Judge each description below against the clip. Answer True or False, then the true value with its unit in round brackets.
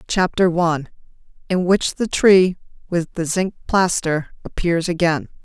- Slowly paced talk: True (120 wpm)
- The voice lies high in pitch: False (175 Hz)